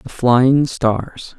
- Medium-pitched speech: No, low, 125 Hz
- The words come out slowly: Yes, slow, 130 wpm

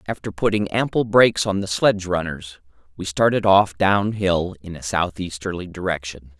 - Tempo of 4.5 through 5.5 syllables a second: Yes, 5.0 syllables/s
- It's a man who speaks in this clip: Yes, male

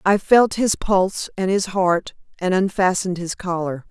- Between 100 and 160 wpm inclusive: No, average, 170 wpm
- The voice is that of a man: No, female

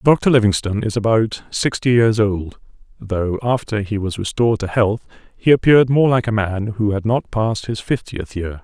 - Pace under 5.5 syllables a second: Yes, 5.0 syllables/s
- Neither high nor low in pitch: No, low, 110 Hz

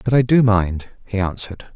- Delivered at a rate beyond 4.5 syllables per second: Yes, 5.1 syllables/s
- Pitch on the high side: No, low, 105 Hz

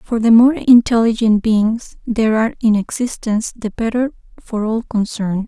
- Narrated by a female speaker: Yes, female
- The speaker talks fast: No, average, 155 wpm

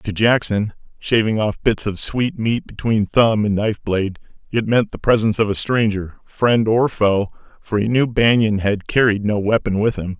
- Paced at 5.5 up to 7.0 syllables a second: No, 4.8 syllables/s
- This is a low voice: Yes, low, 110 Hz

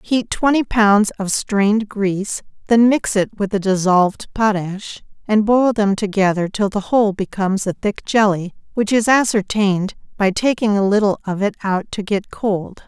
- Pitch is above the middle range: Yes, high, 205 Hz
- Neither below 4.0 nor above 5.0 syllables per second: Yes, 4.7 syllables/s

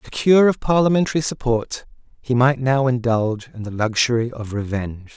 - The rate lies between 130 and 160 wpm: Yes, average, 150 wpm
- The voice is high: No, low, 125 Hz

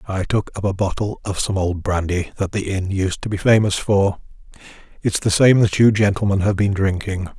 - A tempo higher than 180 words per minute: Yes, fast, 205 wpm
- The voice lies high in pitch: No, low, 100 Hz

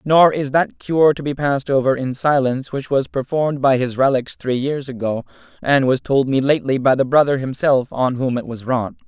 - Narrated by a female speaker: No, male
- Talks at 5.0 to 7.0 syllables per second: Yes, 5.3 syllables/s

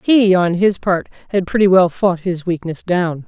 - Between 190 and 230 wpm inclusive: Yes, average, 200 wpm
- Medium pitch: Yes, medium, 180 Hz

